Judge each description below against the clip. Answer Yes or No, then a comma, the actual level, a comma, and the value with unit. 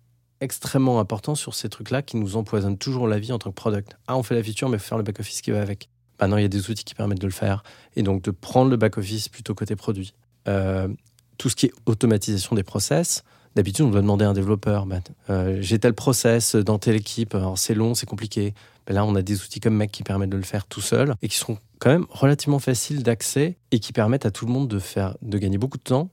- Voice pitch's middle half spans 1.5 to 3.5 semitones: Yes, average, 3.1 semitones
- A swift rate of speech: Yes, fast, 260 wpm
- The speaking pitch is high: No, low, 110 Hz